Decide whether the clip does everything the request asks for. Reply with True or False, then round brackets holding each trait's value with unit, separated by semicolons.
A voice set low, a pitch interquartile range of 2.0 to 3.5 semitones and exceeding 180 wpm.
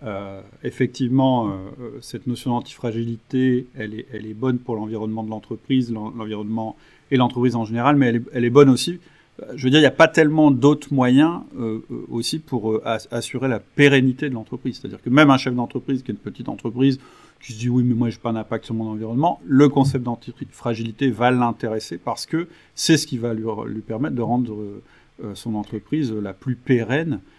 True (120 Hz; 3.0 semitones; 200 wpm)